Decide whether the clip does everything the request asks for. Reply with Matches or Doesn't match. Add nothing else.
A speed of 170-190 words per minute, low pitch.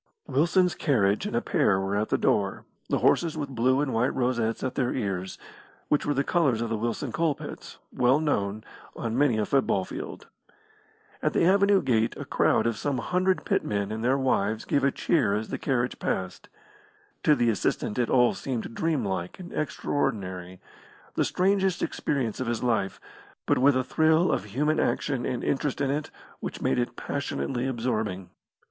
Matches